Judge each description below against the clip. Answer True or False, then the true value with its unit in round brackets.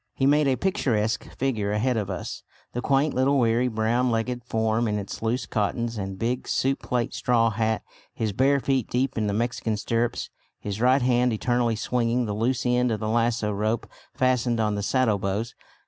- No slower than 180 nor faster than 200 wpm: True (185 wpm)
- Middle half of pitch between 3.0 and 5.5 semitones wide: False (2.5 semitones)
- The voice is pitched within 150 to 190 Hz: False (115 Hz)